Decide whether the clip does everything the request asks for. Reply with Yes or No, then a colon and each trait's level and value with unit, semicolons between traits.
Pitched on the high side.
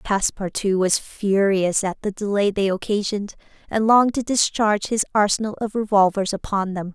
Yes: high, 205 Hz